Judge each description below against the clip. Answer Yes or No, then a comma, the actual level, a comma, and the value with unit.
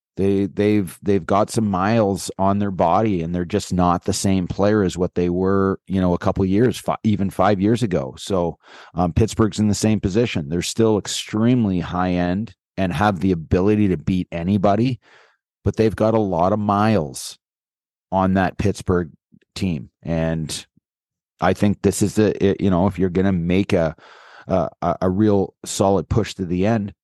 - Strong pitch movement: No, narrow, 2.6 semitones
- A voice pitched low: Yes, low, 100 Hz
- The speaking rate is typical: Yes, average, 180 wpm